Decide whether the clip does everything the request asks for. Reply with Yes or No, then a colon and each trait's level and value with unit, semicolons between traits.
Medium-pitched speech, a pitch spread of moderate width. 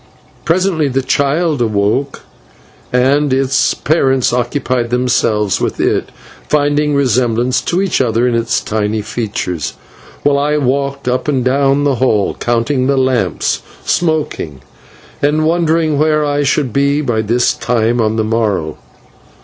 No: low, 130 Hz; average, 3.8 semitones